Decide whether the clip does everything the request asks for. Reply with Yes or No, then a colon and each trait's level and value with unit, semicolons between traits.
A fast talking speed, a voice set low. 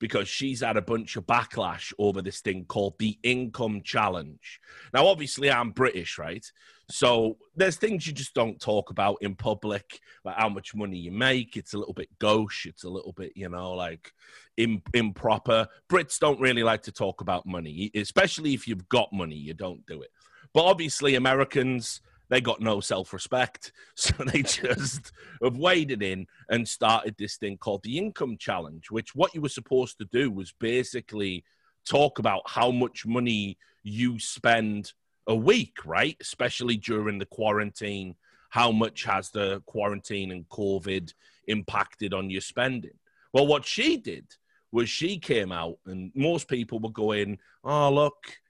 No: average, 170 wpm; low, 110 Hz